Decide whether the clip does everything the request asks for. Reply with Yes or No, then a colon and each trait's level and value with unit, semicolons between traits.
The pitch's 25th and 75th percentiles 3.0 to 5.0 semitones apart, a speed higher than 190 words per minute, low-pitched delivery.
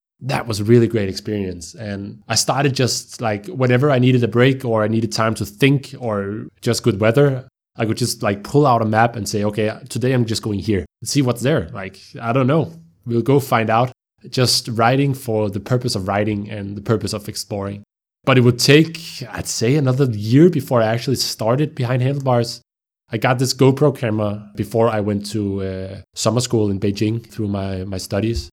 Yes: average, 3.7 semitones; fast, 205 wpm; low, 115 Hz